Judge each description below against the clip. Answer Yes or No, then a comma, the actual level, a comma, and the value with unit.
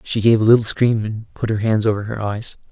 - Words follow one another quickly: Yes, fast, 265 wpm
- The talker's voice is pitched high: No, low, 110 Hz